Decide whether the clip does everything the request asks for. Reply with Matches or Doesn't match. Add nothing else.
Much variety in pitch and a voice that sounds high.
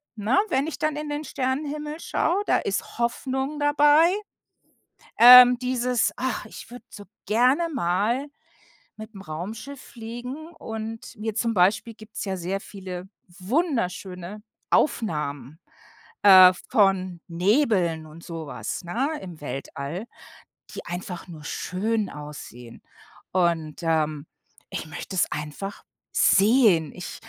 Matches